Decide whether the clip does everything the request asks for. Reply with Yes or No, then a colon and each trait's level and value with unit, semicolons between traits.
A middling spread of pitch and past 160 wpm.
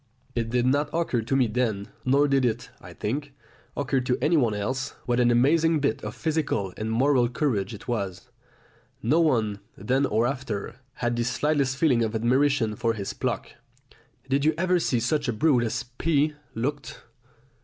Yes: average, 4.1 semitones; average, 175 wpm